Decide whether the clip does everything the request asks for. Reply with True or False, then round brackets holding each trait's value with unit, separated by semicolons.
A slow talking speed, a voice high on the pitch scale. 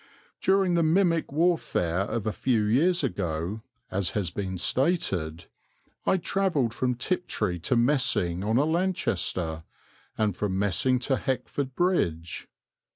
False (130 wpm; 115 Hz)